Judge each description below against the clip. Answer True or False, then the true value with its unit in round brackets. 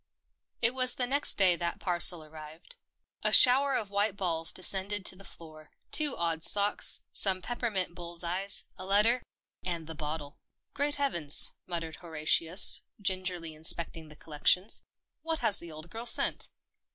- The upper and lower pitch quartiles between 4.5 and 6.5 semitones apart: False (4.1 semitones)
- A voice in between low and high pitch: True (180 Hz)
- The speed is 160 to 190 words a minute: True (165 wpm)